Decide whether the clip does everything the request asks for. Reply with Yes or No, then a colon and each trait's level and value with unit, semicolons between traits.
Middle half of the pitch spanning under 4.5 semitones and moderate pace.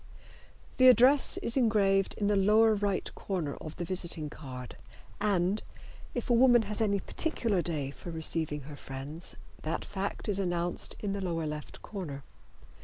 No: average, 4.9 semitones; average, 160 wpm